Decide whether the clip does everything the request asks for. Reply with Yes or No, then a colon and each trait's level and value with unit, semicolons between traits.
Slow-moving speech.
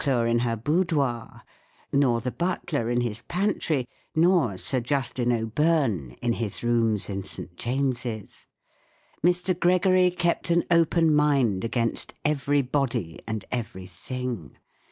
Yes: slow, 125 wpm